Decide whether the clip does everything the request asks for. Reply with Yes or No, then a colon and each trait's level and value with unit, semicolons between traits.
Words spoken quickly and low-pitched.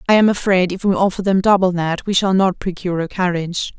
No: fast, 240 wpm; medium, 185 Hz